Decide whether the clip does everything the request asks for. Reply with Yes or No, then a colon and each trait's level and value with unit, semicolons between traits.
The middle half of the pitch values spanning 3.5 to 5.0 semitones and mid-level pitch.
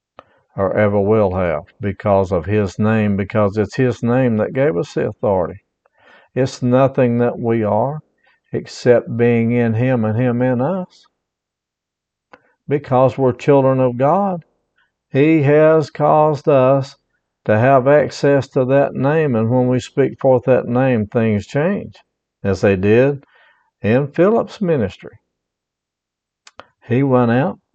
No: average, 4.0 semitones; low, 130 Hz